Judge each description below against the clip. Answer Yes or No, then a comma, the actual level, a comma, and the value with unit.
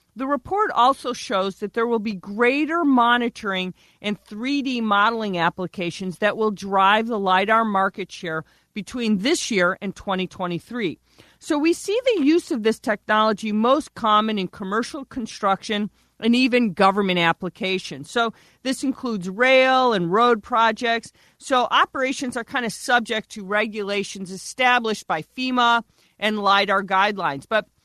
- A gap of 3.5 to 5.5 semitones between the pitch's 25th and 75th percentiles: Yes, average, 4.1 semitones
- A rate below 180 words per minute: Yes, average, 140 wpm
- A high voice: Yes, high, 220 Hz